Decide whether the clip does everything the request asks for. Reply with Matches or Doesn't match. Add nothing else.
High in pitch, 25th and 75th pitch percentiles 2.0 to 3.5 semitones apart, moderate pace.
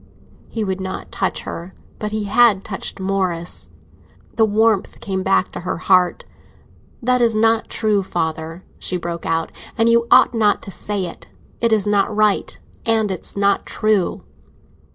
Matches